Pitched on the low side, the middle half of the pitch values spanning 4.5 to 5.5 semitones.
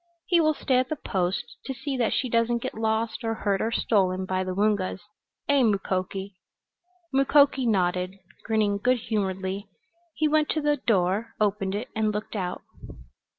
No: high, 215 Hz; average, 4.8 semitones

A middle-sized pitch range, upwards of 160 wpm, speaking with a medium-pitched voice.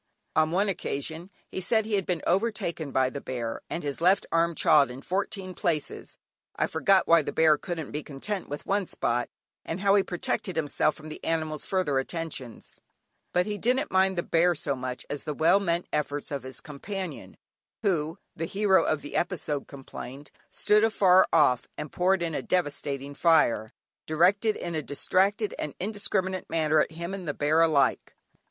Yes: average, 4.5 semitones; average, 180 wpm; medium, 165 Hz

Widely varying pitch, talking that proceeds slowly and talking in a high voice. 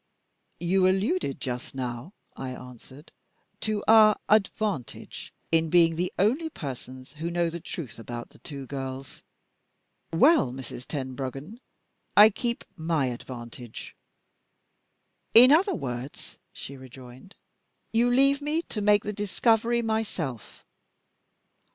No: wide, 8.7 semitones; slow, 115 wpm; medium, 165 Hz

